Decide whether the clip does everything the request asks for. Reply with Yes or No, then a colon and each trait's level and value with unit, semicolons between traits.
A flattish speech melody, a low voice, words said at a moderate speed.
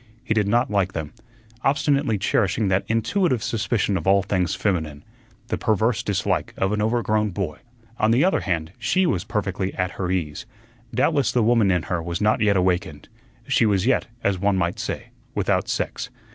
No: average, 3.9 semitones; low, 100 Hz; average, 180 wpm